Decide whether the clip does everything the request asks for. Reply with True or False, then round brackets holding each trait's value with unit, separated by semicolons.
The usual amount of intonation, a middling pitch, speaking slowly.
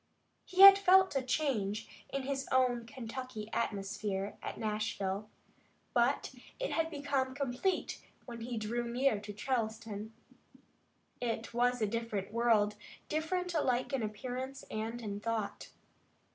False (4.0 semitones; 240 Hz; 130 wpm)